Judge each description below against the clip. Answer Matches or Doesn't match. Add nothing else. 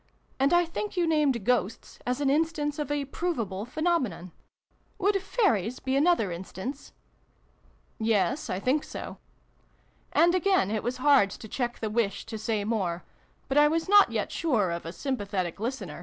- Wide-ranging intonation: Matches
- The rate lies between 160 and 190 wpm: Matches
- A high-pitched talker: Matches